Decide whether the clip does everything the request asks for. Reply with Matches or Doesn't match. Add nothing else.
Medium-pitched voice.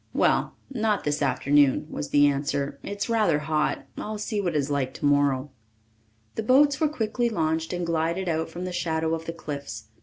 Matches